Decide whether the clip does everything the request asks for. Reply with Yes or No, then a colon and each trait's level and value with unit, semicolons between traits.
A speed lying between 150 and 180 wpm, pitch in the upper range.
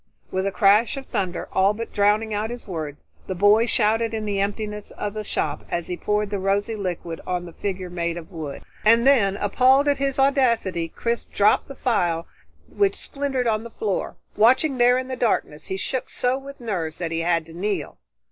No: fast, 205 wpm; high, 210 Hz